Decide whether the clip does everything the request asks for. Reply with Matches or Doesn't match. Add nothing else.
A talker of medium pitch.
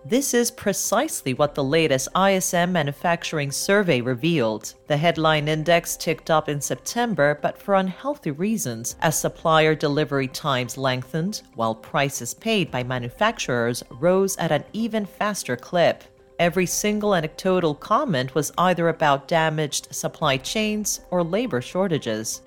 Matches